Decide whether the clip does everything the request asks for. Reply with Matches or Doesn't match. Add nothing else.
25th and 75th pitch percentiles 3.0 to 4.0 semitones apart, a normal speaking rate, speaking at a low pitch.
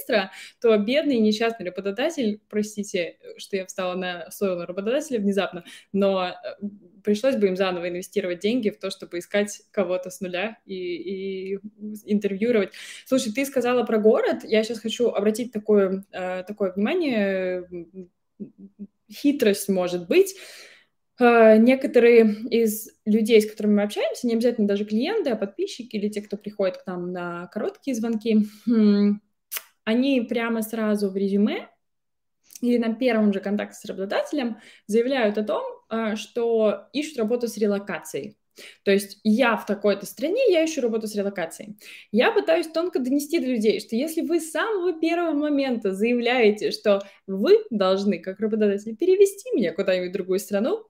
Doesn't match